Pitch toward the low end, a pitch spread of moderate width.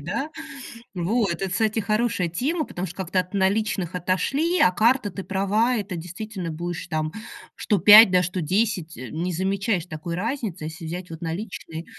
No: medium, 185 Hz; average, 4.0 semitones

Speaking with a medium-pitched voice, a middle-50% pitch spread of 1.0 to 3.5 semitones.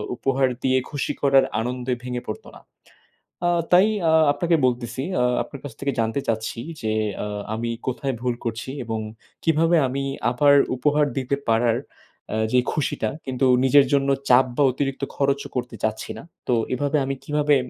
No: low, 130 Hz; average, 2.8 semitones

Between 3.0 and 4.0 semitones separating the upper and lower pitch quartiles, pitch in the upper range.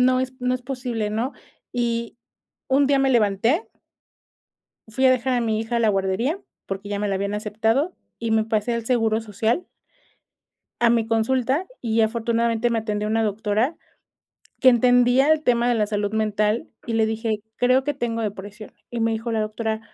No: narrow, 2.4 semitones; high, 230 Hz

